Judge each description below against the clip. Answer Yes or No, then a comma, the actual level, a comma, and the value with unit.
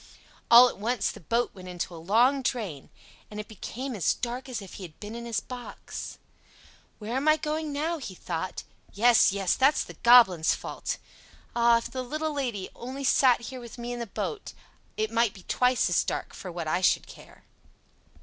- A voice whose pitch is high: Yes, high, 235 Hz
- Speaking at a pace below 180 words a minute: No, average, 200 wpm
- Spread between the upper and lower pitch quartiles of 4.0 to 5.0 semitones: Yes, average, 4.3 semitones